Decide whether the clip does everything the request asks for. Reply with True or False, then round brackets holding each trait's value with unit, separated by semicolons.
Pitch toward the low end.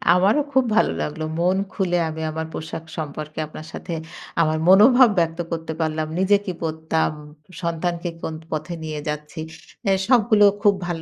False (165 Hz)